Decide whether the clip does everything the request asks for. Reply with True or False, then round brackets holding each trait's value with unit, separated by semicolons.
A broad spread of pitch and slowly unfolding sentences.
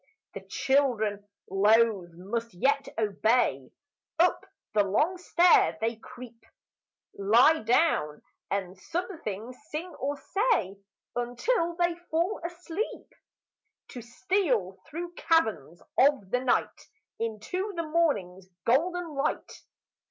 True (8.4 semitones; 105 wpm)